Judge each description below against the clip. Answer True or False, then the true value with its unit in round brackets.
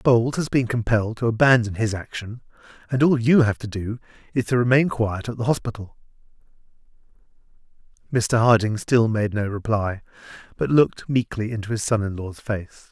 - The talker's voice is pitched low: True (115 Hz)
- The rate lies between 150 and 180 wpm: True (165 wpm)